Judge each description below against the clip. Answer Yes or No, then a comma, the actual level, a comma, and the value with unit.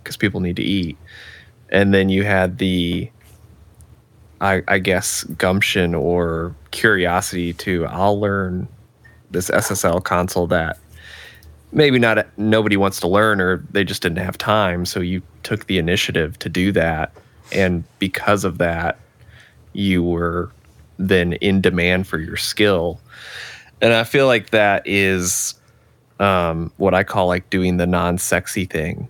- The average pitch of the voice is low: Yes, very low, 95 Hz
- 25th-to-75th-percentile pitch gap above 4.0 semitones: No, narrow, 2.5 semitones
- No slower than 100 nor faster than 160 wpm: Yes, average, 145 wpm